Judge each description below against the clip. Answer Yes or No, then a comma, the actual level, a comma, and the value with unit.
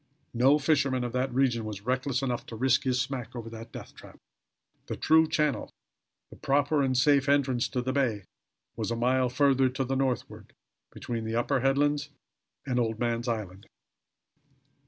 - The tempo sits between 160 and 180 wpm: Yes, average, 170 wpm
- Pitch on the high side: No, low, 130 Hz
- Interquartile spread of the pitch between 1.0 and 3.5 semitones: Yes, narrow, 2.6 semitones